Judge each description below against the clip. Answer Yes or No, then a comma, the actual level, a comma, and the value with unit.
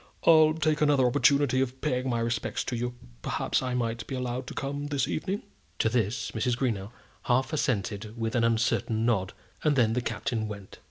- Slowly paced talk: No, average, 185 wpm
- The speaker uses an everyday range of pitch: Yes, average, 3.3 semitones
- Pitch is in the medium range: No, low, 125 Hz